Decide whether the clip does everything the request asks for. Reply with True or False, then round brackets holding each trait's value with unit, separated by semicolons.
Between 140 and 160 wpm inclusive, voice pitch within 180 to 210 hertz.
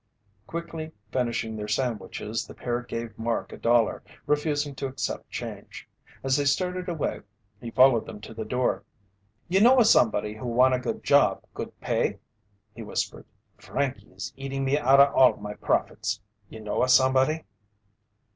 False (155 wpm; 130 Hz)